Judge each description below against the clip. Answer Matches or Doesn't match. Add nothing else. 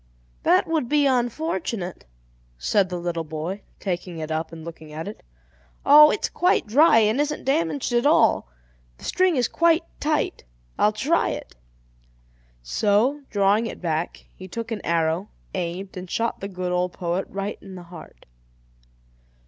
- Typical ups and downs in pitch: Doesn't match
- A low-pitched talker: Doesn't match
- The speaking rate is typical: Matches